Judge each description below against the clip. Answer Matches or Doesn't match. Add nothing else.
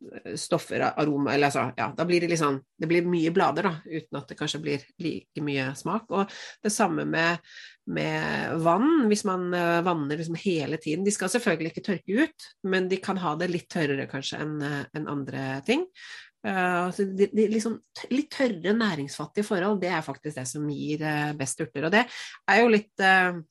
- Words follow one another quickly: Doesn't match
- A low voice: Doesn't match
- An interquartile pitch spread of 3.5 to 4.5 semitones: Doesn't match